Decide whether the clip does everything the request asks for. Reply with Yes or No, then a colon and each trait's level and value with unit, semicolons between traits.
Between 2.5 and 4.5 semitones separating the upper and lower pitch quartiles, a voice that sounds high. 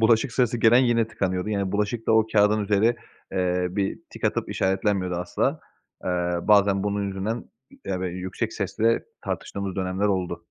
No: average, 3.0 semitones; low, 100 Hz